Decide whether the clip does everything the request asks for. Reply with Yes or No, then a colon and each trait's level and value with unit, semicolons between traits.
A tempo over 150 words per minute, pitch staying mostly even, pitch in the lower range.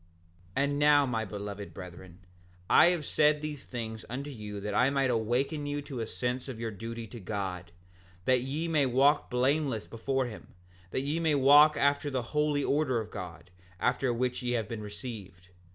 No: average, 185 wpm; average, 4.8 semitones; low, 125 Hz